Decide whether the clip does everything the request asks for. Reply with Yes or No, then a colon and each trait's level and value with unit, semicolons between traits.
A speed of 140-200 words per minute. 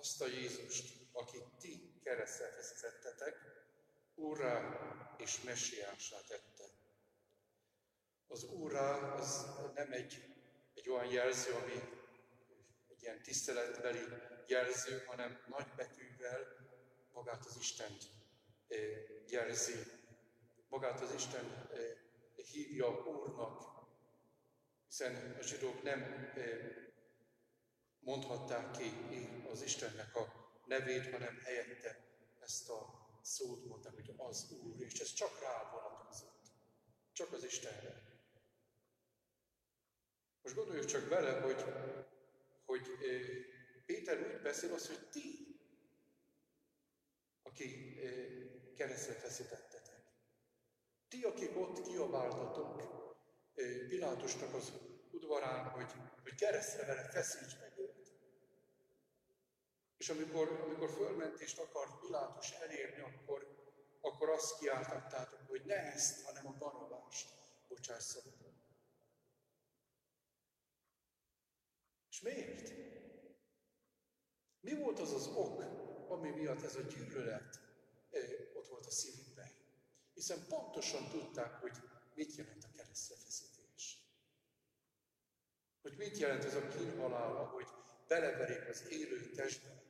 No: slow, 100 wpm